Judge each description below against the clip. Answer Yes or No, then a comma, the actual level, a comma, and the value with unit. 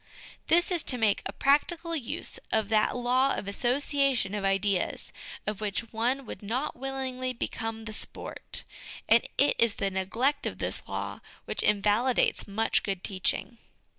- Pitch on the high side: Yes, high, 230 Hz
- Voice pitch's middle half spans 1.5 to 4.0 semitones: No, average, 4.5 semitones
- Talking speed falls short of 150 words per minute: No, average, 160 wpm